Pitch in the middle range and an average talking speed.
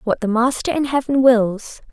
No: high, 245 Hz; average, 190 wpm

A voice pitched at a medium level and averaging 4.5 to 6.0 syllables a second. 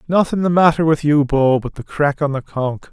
Yes: medium, 150 Hz; 5.1 syllables/s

